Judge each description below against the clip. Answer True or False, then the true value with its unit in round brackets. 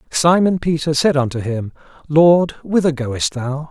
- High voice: False (150 Hz)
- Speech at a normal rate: True (145 wpm)